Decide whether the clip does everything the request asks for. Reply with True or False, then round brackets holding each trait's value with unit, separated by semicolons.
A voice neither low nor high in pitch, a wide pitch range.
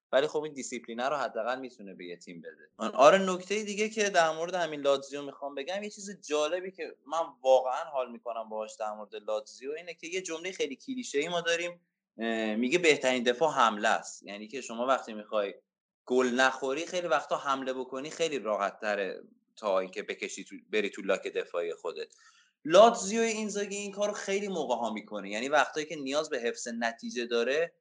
True (160 Hz; 8.8 semitones)